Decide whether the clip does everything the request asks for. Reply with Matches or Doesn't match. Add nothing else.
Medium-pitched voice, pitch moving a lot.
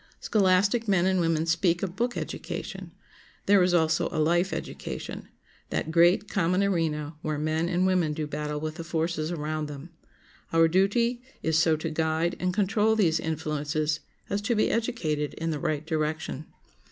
Doesn't match